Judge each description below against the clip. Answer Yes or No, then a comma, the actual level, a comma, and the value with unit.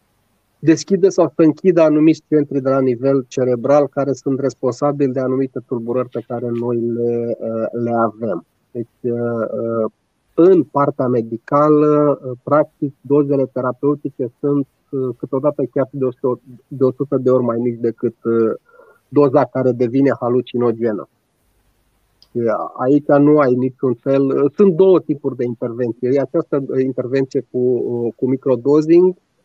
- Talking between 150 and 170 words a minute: No, average, 120 wpm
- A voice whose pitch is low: Yes, low, 130 Hz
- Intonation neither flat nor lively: Yes, average, 3.3 semitones